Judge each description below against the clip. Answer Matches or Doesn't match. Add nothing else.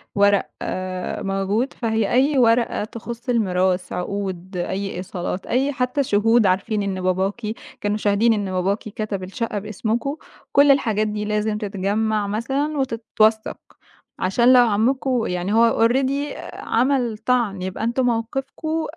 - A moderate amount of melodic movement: Matches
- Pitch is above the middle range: Matches